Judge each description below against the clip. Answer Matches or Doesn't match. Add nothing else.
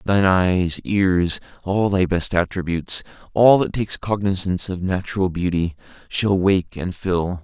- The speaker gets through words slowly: Matches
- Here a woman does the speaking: Doesn't match